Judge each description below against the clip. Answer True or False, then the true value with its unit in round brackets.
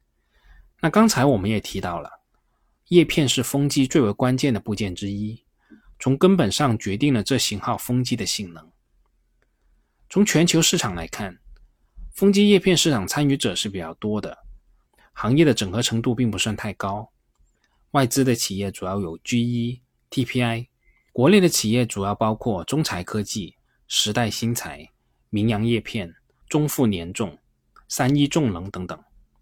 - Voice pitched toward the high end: False (120 Hz)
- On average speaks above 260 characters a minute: False (235 characters per minute)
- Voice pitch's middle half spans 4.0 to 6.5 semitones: True (5.5 semitones)